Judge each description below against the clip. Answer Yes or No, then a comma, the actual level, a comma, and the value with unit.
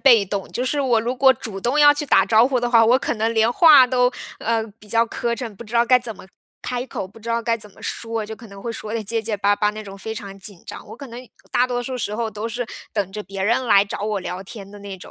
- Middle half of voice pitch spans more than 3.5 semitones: No, average, 2.9 semitones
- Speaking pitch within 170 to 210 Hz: No, high, 225 Hz